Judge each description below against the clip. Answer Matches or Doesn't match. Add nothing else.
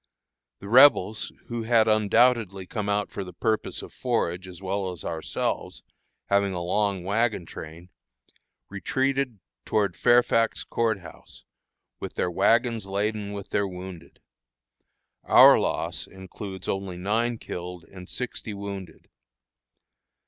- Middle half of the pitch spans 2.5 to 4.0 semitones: Matches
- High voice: Doesn't match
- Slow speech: Matches